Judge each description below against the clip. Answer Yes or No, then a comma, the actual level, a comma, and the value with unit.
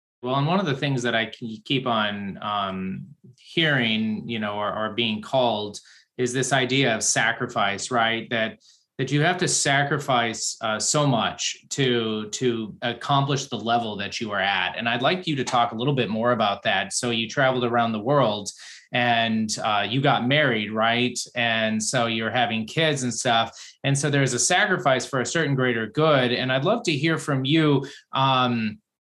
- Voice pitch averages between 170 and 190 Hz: No, low, 120 Hz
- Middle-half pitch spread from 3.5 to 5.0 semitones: Yes, average, 3.8 semitones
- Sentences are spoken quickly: No, average, 190 wpm